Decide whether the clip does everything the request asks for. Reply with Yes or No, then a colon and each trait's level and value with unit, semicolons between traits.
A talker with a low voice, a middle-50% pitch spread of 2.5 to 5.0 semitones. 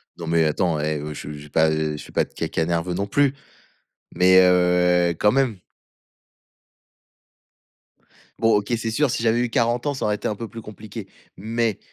No: very low, 95 Hz; wide, 5.4 semitones